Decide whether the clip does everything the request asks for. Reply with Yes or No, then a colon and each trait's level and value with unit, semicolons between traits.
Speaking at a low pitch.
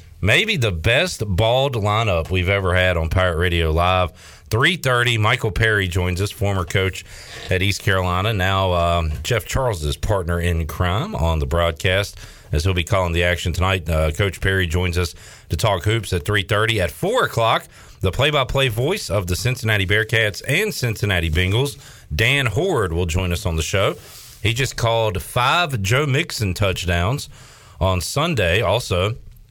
Yes: low, 100 Hz